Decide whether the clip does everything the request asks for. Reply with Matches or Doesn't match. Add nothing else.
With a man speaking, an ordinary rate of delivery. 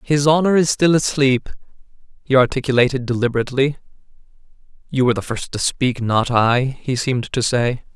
Matches